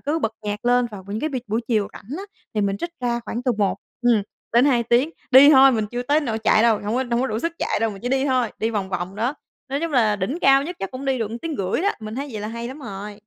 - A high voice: Yes, high, 235 Hz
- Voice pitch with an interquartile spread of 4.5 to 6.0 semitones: No, average, 4.1 semitones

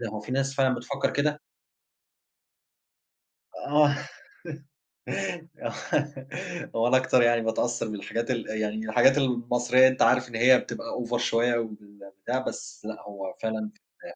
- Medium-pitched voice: No, low, 120 Hz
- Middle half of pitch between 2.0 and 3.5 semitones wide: Yes, average, 2.9 semitones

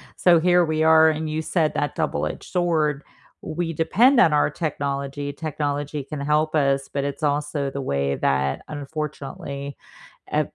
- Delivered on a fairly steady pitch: Yes, narrow, 2.2 semitones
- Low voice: No, medium, 150 Hz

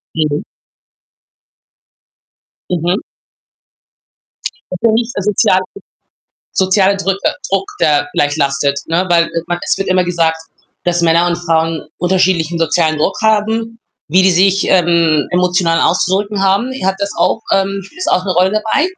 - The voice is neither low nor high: Yes, medium, 180 Hz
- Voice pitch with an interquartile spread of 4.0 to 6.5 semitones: No, average, 2.8 semitones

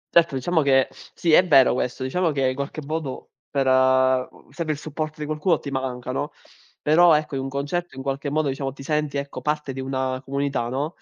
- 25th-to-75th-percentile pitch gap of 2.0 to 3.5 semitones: Yes, narrow, 2.6 semitones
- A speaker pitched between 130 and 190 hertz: Yes, medium, 140 Hz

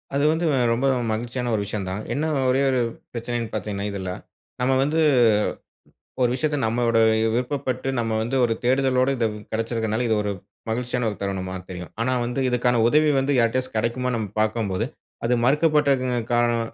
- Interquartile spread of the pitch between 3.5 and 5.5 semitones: No, narrow, 2.6 semitones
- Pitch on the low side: Yes, low, 120 Hz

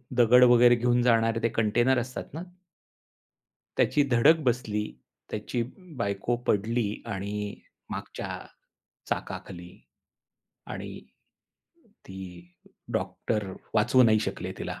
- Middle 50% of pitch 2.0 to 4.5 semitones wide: Yes, average, 2.9 semitones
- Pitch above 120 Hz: No, low, 115 Hz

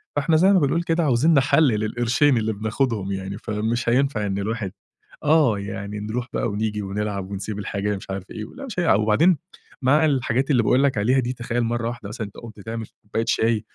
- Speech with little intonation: No, average, 4.5 semitones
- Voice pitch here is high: No, low, 115 Hz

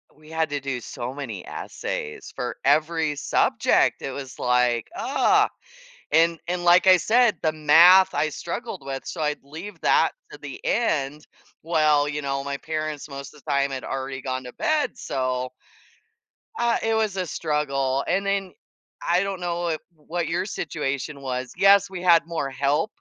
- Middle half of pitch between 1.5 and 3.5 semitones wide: No, average, 4.3 semitones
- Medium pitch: Yes, medium, 155 Hz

